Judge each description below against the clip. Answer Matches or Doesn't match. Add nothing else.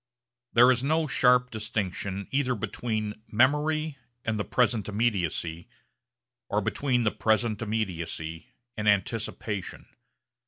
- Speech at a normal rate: Doesn't match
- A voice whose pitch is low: Matches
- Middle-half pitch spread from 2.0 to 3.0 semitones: Doesn't match